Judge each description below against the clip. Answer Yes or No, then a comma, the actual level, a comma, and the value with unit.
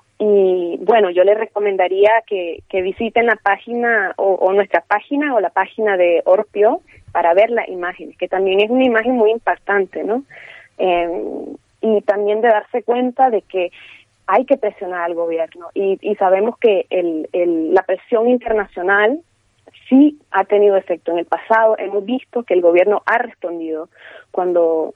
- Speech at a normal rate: Yes, average, 165 wpm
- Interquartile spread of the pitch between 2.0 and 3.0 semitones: No, average, 3.8 semitones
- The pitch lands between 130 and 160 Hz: No, high, 205 Hz